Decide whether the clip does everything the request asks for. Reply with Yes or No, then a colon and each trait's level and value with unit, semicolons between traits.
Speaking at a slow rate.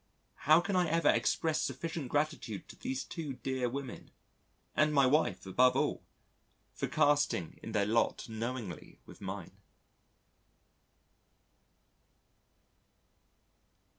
Yes: slow, 105 wpm